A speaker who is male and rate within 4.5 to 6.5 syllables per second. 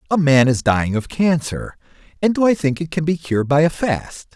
Yes: male; 5.5 syllables/s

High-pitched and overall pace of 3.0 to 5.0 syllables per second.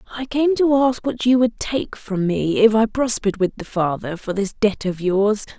Yes: high, 220 Hz; 4.7 syllables/s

